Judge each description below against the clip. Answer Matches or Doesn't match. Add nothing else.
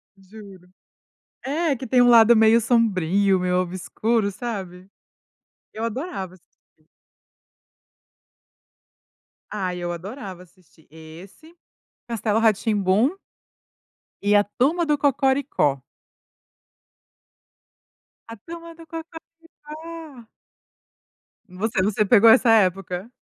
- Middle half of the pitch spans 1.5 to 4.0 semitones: Doesn't match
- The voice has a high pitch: Matches